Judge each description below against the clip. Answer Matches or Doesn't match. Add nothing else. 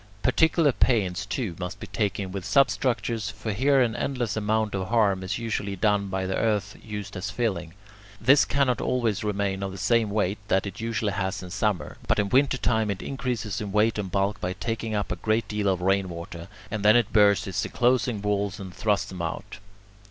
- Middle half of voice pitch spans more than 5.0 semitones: Doesn't match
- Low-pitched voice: Matches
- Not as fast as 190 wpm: Doesn't match